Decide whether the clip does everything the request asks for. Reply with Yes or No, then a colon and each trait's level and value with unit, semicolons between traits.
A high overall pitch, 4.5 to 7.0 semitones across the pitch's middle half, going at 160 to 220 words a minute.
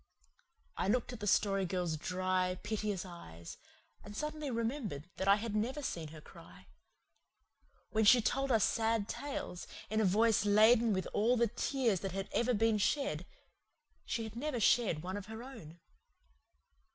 No: high, 215 Hz; average, 4.0 semitones; average, 165 wpm